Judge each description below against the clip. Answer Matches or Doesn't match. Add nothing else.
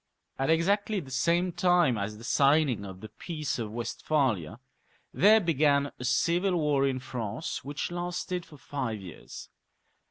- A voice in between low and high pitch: Matches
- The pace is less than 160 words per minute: Matches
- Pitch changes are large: Matches